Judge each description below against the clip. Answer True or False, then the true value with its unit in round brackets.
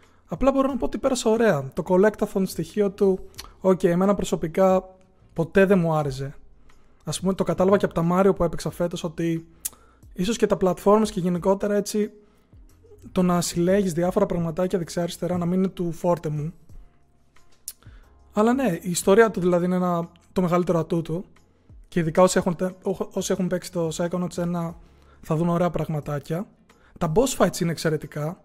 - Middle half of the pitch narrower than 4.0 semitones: True (2.7 semitones)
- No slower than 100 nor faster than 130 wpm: False (170 wpm)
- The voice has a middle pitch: True (180 Hz)